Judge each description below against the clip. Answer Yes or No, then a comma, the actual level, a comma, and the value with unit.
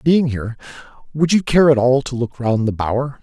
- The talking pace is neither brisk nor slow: No, fast, 225 wpm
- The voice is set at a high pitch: No, low, 130 Hz